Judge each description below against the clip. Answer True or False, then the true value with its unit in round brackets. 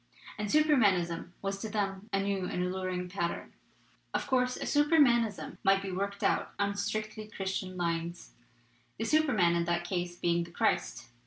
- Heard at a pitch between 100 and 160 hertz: False (195 Hz)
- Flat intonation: False (3.5 semitones)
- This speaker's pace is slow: False (160 wpm)